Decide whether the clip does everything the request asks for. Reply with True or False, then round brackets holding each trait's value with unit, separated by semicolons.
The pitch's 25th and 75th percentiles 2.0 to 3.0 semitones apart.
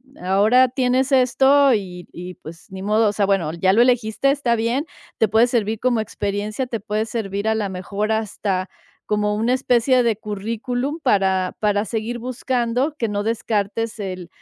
False (3.5 semitones)